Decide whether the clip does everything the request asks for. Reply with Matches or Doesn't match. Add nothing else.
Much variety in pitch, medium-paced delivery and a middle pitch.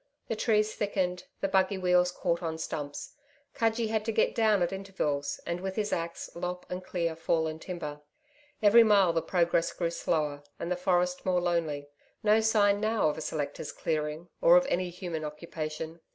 Doesn't match